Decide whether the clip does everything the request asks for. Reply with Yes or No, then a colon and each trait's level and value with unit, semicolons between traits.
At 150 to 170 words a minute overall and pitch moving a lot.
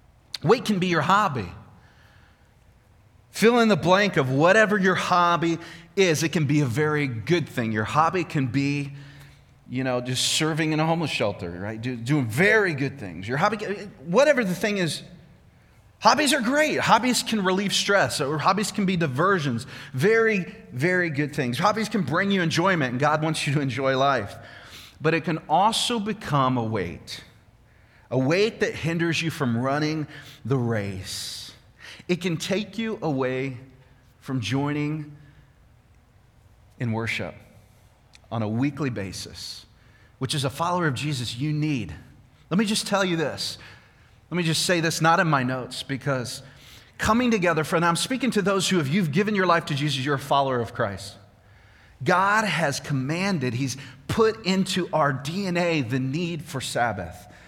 Yes: average, 165 wpm; wide, 6.8 semitones